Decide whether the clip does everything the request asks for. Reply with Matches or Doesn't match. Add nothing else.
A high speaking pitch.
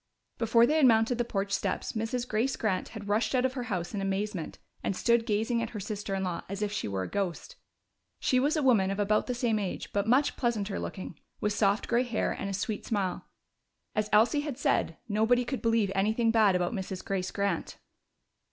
Matches